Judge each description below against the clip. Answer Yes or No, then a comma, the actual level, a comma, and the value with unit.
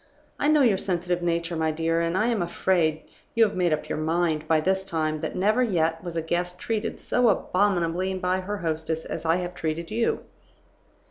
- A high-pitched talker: No, medium, 175 Hz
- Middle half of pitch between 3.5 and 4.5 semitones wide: No, average, 2.7 semitones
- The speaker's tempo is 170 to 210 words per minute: Yes, average, 200 wpm